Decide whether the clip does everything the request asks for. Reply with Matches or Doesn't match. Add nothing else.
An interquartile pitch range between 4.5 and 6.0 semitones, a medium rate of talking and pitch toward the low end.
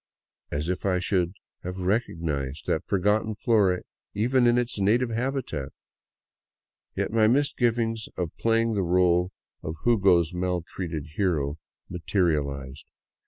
Doesn't match